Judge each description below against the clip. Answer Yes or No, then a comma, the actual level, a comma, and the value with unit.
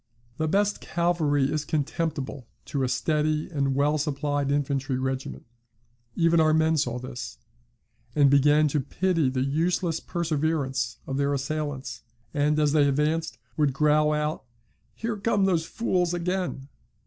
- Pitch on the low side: No, medium, 150 Hz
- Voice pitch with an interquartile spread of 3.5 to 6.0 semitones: No, average, 2.9 semitones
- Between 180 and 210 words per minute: No, average, 140 wpm